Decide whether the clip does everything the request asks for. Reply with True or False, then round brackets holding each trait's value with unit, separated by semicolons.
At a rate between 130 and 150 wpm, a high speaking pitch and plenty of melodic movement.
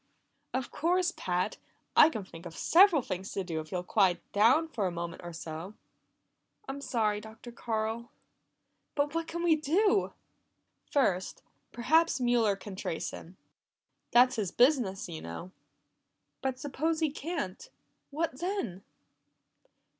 True (140 wpm; 235 Hz; 8.7 semitones)